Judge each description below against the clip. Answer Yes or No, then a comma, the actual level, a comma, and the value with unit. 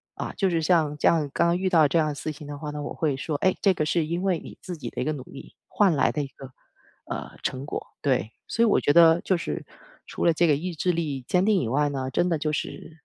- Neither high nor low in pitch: Yes, medium, 155 Hz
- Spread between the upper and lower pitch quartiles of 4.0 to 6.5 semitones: No, average, 3.2 semitones